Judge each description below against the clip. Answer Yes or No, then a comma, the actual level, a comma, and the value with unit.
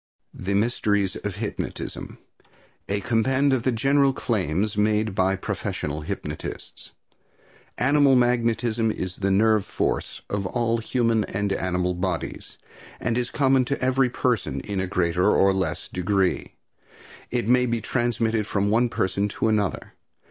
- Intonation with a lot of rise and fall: No, average, 3.9 semitones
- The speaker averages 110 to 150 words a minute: Yes, average, 140 wpm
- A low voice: Yes, low, 110 Hz